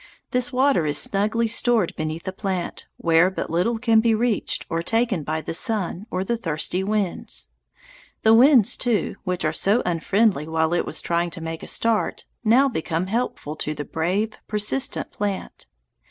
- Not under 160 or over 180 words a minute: Yes, average, 170 wpm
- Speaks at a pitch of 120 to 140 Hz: No, high, 195 Hz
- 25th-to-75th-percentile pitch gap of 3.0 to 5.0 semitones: No, wide, 5.5 semitones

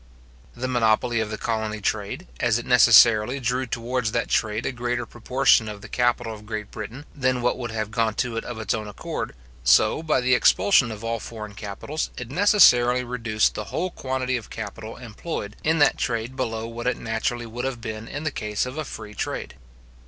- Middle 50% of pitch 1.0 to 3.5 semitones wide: Yes, narrow, 2.5 semitones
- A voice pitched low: Yes, low, 115 Hz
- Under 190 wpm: No, average, 200 wpm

